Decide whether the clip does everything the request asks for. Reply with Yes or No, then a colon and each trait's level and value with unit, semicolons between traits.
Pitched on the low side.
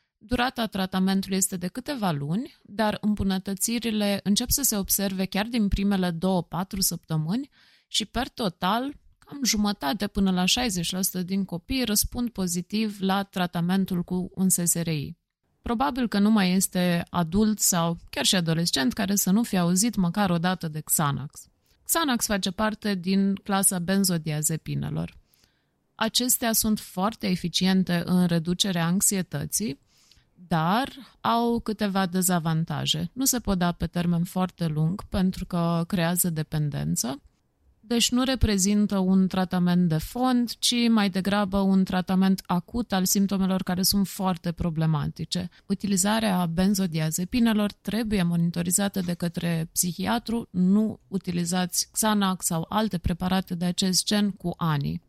No: high, 190 Hz